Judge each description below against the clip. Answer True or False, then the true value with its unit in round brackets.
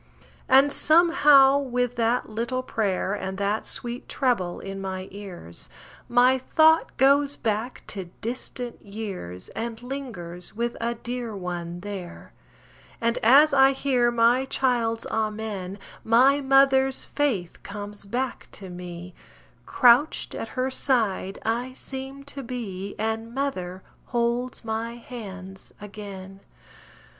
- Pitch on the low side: False (230 Hz)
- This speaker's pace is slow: True (120 wpm)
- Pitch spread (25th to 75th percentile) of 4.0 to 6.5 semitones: True (4.8 semitones)